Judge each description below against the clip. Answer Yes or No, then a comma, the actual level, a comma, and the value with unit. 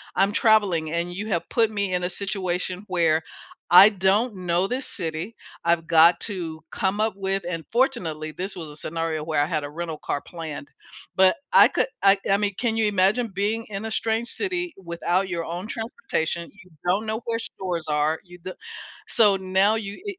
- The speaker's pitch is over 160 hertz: Yes, medium, 185 Hz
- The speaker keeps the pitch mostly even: No, average, 4.0 semitones